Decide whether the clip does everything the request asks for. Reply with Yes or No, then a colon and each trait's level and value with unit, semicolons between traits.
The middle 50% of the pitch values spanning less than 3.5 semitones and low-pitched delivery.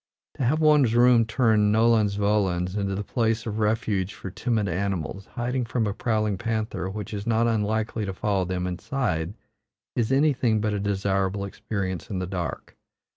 Yes: average, 2.9 semitones; low, 105 Hz